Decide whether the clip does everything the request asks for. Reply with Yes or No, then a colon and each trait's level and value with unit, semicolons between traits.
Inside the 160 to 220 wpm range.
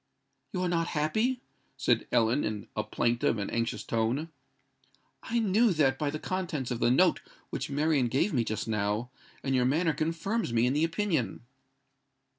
Yes: average, 170 wpm